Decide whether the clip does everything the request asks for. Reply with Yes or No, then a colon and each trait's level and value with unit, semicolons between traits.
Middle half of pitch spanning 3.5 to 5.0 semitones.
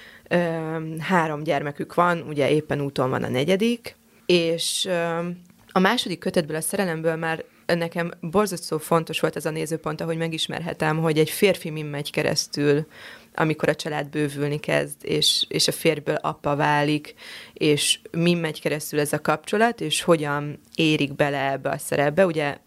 No: narrow, 2.5 semitones